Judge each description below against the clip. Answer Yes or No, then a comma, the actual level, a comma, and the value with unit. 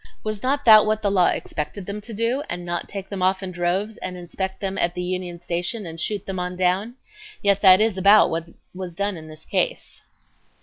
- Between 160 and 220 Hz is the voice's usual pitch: Yes, high, 190 Hz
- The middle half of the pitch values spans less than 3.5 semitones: Yes, average, 2.8 semitones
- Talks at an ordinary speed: No, fast, 220 wpm